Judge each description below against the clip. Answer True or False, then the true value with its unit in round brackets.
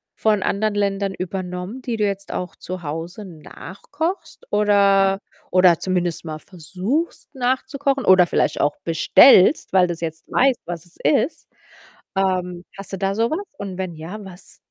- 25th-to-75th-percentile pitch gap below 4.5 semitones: True (3.2 semitones)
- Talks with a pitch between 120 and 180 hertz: False (195 Hz)